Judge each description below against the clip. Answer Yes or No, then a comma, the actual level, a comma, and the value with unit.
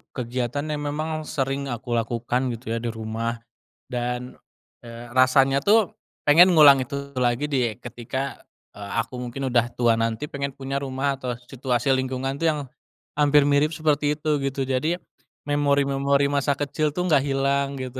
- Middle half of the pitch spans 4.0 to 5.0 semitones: No, average, 2.8 semitones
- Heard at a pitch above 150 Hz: No, low, 135 Hz